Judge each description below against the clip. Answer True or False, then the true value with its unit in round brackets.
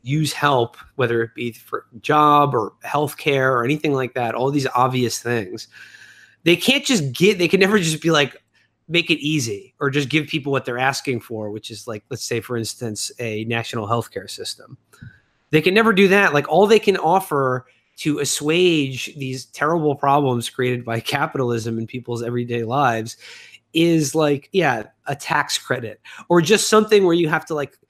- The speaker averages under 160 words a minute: False (185 wpm)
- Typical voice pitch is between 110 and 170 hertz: True (140 Hz)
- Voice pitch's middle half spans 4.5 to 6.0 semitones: True (4.9 semitones)